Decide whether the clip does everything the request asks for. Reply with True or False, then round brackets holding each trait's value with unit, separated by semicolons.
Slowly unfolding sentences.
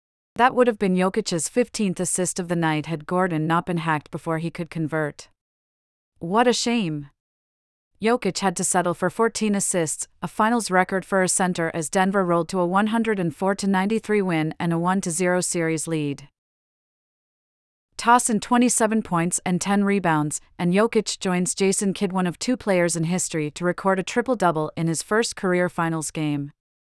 False (175 wpm)